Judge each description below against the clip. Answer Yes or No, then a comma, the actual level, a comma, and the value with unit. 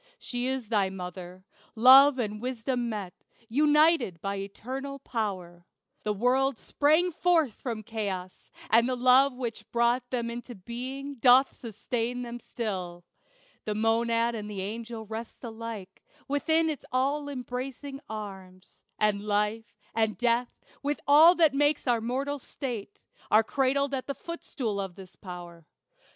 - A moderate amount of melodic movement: Yes, average, 4.3 semitones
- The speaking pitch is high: Yes, high, 235 Hz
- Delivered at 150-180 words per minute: No, average, 140 wpm